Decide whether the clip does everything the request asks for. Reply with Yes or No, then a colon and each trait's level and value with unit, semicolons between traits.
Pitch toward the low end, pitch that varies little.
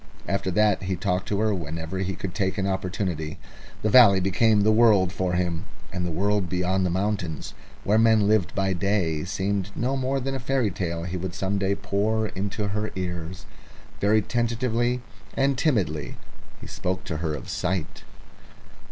No: very low, 95 Hz; average, 3.1 semitones